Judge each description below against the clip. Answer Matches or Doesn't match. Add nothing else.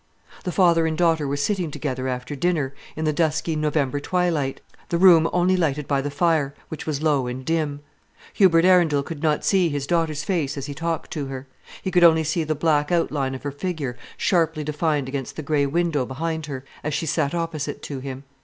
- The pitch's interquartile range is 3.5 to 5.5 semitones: Doesn't match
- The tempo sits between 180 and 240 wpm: Matches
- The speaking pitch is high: Doesn't match